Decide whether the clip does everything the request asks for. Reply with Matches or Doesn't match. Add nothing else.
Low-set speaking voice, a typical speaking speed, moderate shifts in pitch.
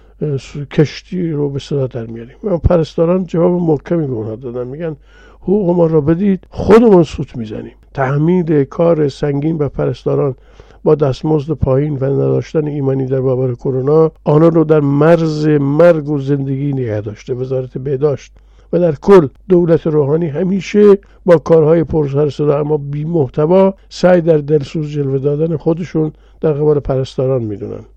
Doesn't match